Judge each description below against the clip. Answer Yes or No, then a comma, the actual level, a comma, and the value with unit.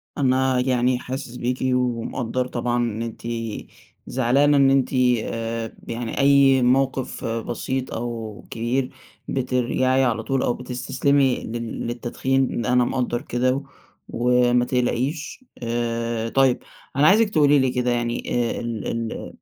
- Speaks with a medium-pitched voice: No, low, 125 Hz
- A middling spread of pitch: No, narrow, 2.0 semitones